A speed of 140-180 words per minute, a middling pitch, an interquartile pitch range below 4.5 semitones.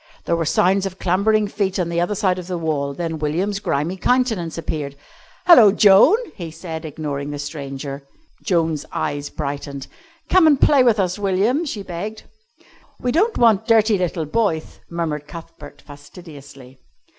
No: average, 155 wpm; medium, 175 Hz; wide, 5.5 semitones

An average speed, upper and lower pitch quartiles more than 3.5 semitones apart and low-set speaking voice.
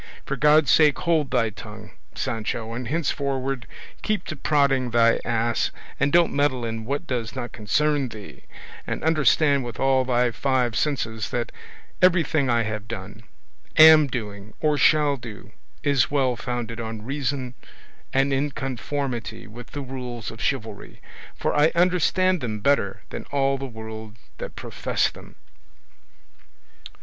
Yes: average, 145 wpm; average, 4.0 semitones; low, 130 Hz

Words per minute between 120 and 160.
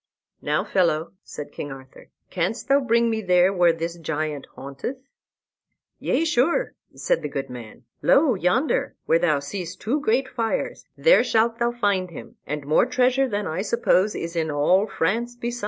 No: average, 170 wpm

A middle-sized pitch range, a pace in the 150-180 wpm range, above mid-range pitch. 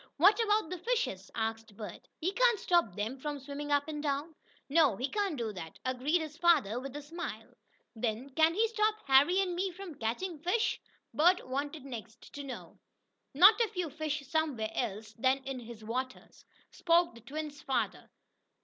No: wide, 6.0 semitones; average, 175 wpm; very high, 290 Hz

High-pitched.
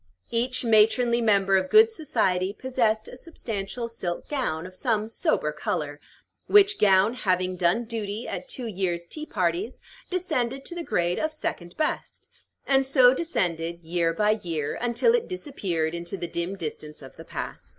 Yes: high, 210 Hz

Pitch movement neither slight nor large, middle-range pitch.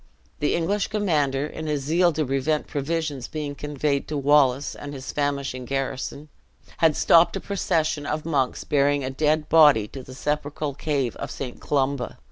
No: narrow, 2.2 semitones; medium, 145 Hz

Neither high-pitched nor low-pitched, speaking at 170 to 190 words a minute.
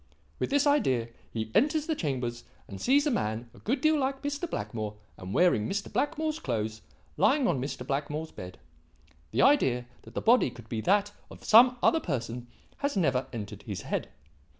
Yes: medium, 155 Hz; average, 180 wpm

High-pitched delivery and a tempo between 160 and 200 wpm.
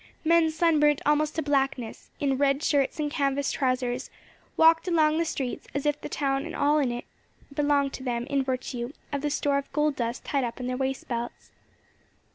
Yes: very high, 280 Hz; average, 195 wpm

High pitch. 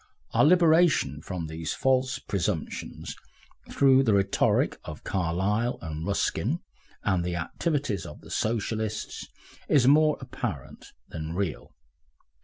No: low, 100 Hz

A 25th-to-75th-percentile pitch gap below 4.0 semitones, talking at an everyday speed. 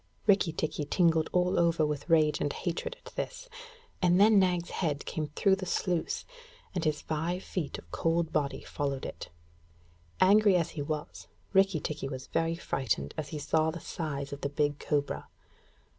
Yes: average, 3.4 semitones; average, 175 wpm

